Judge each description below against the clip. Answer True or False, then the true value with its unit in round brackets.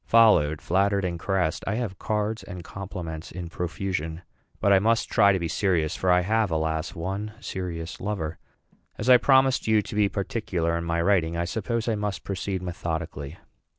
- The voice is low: True (95 Hz)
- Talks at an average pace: True (180 wpm)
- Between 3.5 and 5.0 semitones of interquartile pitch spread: True (3.8 semitones)